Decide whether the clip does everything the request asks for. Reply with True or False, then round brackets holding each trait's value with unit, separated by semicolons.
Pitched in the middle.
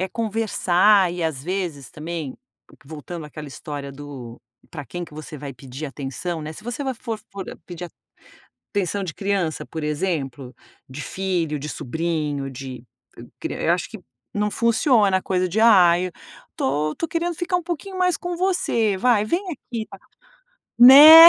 True (180 Hz)